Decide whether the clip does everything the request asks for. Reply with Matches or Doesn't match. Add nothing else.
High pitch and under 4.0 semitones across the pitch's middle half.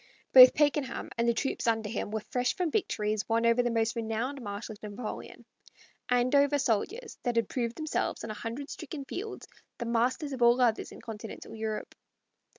Matches